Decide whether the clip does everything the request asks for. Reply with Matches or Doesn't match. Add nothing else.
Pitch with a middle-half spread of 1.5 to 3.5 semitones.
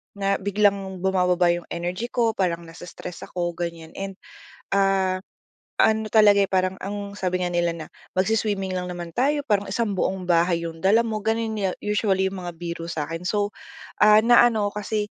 Matches